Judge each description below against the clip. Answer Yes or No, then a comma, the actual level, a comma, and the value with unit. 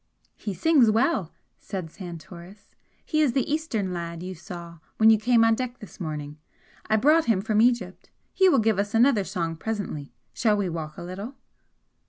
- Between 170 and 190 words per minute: Yes, average, 180 wpm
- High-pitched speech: Yes, high, 205 Hz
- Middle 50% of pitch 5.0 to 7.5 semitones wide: Yes, wide, 5.4 semitones